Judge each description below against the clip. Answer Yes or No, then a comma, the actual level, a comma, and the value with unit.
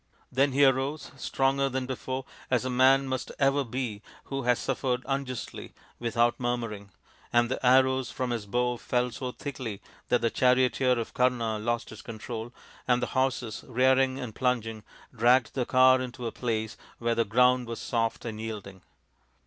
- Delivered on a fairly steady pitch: Yes, narrow, 2.0 semitones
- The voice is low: Yes, low, 125 Hz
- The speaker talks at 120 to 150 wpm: No, average, 165 wpm